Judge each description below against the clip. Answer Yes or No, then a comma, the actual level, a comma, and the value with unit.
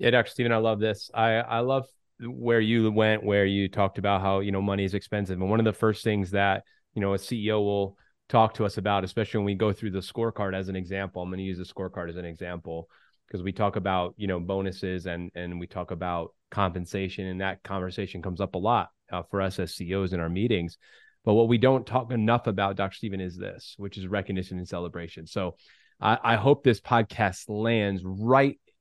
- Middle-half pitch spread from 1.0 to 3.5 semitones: Yes, average, 3.0 semitones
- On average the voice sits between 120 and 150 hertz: No, low, 100 Hz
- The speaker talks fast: Yes, fast, 225 wpm